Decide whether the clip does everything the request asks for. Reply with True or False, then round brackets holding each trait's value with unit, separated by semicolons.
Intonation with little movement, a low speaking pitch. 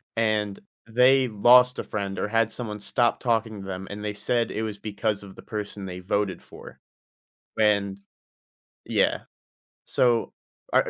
True (2.3 semitones; 105 Hz)